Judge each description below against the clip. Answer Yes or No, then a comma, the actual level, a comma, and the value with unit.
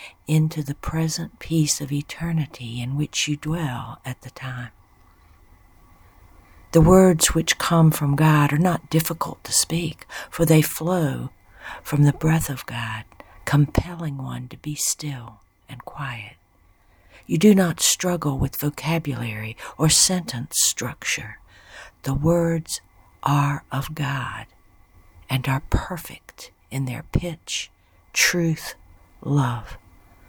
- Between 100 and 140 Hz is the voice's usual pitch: Yes, low, 135 Hz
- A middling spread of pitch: No, wide, 7.4 semitones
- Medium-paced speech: No, slow, 120 wpm